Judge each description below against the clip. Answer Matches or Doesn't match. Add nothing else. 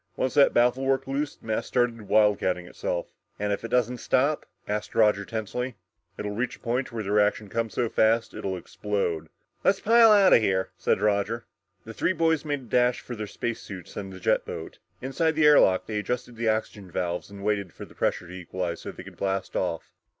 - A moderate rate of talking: Doesn't match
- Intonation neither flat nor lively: Matches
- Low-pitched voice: Matches